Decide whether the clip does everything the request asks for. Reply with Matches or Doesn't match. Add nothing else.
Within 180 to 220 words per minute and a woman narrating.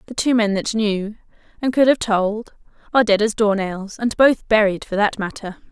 Matches